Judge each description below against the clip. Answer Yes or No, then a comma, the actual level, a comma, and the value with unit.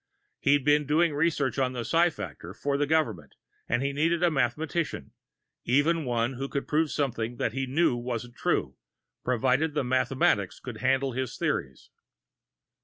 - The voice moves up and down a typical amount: Yes, average, 3.6 semitones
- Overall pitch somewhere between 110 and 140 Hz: Yes, low, 135 Hz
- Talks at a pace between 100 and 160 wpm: Yes, average, 155 wpm